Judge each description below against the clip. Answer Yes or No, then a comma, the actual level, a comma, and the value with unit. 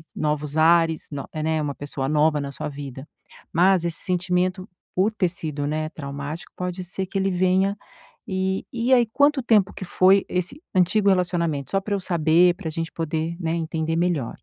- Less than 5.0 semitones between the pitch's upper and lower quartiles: Yes, average, 3.4 semitones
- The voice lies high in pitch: No, medium, 170 Hz